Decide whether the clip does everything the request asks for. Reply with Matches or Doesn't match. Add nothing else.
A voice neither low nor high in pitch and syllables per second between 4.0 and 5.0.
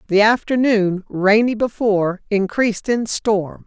Doesn't match